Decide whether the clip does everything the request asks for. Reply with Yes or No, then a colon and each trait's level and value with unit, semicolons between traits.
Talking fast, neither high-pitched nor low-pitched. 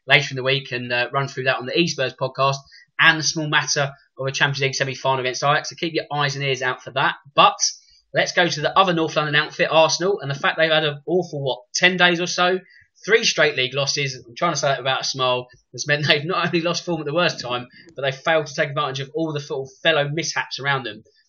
Yes: fast, 255 wpm; medium, 150 Hz